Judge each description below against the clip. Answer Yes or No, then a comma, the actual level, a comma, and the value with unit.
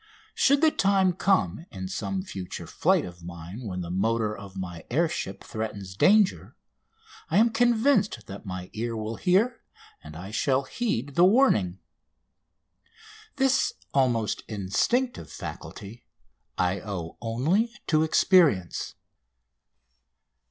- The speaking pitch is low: Yes, low, 115 Hz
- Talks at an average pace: No, slow, 125 wpm